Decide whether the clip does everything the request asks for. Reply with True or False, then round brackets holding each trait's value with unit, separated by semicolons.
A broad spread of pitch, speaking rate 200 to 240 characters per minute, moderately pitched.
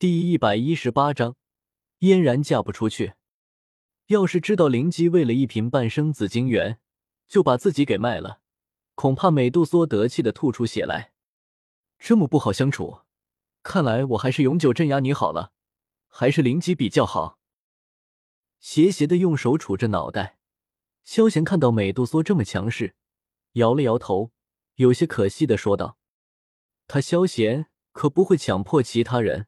False (7.0 semitones; 230 characters per minute; 130 Hz)